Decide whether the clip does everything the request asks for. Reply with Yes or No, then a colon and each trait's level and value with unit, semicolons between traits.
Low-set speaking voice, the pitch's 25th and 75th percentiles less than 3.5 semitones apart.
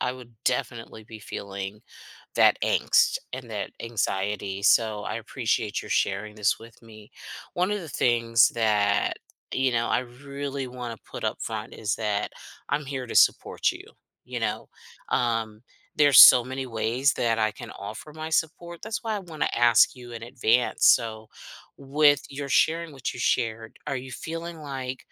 No: low, 120 Hz; average, 4.1 semitones